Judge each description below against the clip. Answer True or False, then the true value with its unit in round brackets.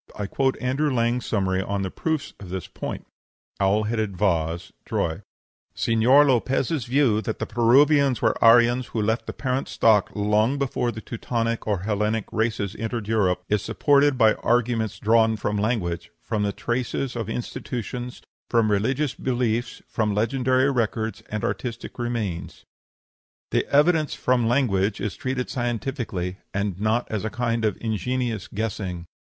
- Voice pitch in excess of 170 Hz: False (115 Hz)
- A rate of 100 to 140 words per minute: False (150 wpm)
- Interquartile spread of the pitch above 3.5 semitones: False (3.2 semitones)